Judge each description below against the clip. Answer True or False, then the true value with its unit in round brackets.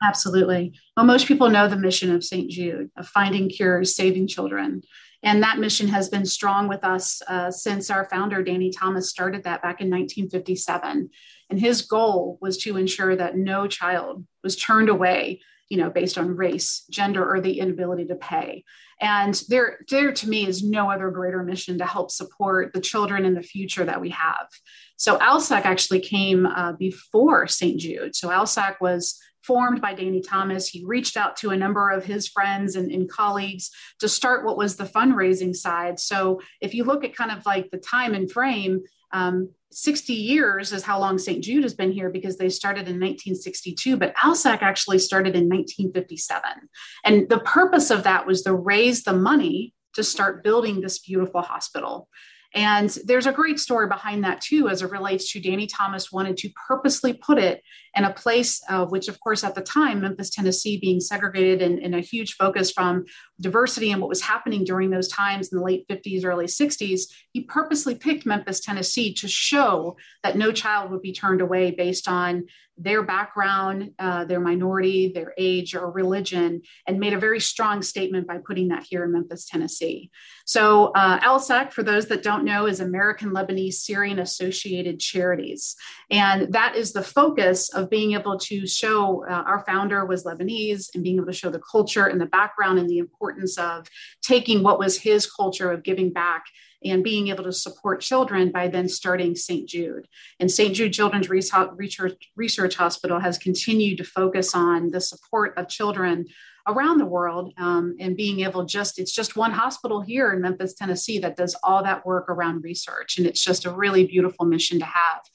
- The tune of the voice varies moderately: False (2.2 semitones)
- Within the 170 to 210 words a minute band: True (190 wpm)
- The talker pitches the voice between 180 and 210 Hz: True (190 Hz)